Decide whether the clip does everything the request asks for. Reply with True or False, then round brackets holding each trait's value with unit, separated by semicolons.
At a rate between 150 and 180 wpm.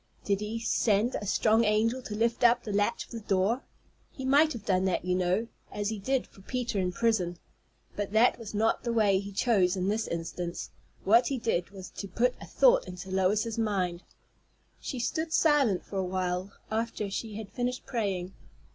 False (195 wpm)